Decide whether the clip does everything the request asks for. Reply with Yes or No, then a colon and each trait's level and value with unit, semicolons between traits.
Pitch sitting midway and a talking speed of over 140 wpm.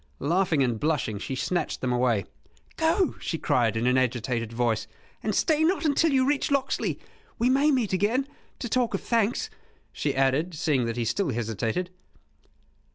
Yes: medium, 160 Hz; average, 160 wpm